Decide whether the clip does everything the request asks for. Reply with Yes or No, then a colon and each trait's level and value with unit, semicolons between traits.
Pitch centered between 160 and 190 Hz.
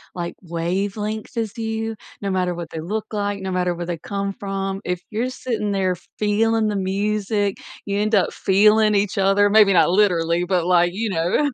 No: high, 200 Hz